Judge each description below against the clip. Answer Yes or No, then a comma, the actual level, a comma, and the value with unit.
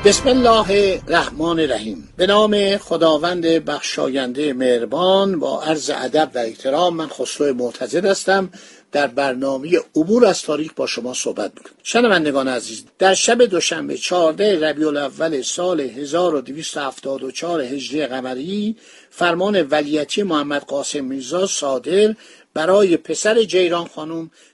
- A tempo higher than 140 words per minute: No, average, 120 wpm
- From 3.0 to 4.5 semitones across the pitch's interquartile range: No, average, 5.1 semitones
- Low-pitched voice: No, medium, 165 Hz